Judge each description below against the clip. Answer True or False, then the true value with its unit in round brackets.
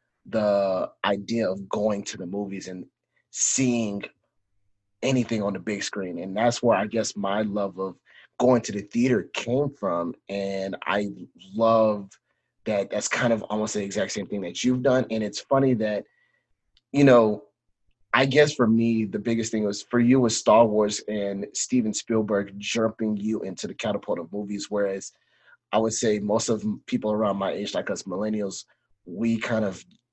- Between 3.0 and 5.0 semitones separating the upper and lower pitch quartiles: False (2.4 semitones)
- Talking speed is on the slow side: False (175 wpm)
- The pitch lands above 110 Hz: False (105 Hz)